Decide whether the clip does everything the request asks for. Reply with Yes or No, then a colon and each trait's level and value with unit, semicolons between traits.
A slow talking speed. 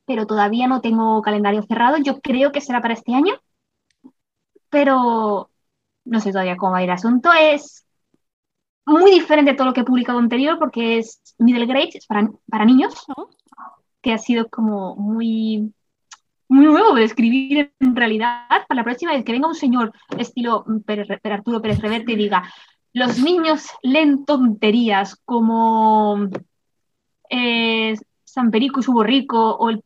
No: average, 165 wpm